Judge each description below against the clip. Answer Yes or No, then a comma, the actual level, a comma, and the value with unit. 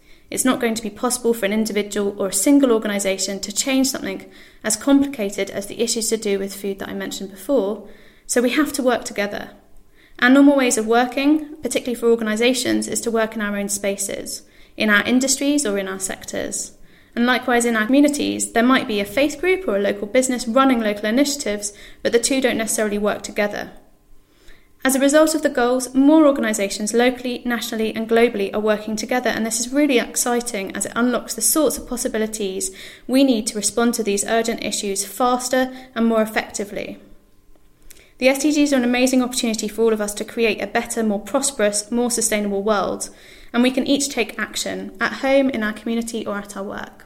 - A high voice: Yes, high, 230 Hz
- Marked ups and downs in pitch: No, average, 3.7 semitones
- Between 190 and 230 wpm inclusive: Yes, average, 200 wpm